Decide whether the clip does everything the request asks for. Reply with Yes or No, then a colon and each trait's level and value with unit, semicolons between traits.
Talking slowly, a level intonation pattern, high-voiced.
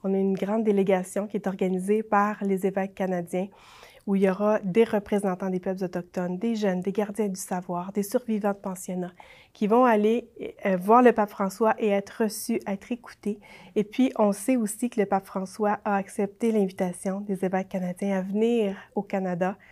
No: average, 190 wpm; narrow, 2.0 semitones; high, 200 Hz